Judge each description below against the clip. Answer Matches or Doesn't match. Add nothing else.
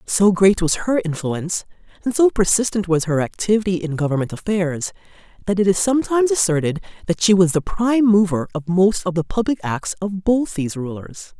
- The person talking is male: Doesn't match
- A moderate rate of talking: Matches